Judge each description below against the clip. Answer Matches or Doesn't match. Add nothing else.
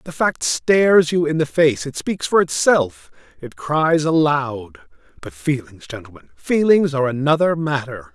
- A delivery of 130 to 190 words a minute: Matches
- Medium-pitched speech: Matches